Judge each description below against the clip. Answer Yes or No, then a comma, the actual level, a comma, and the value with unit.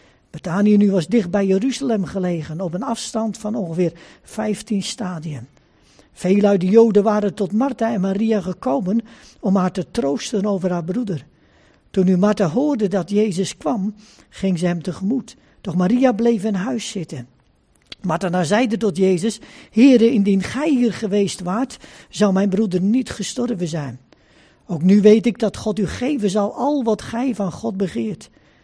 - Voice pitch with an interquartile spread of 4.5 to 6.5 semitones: No, average, 3.6 semitones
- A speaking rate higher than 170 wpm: No, average, 165 wpm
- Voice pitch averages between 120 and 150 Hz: No, high, 205 Hz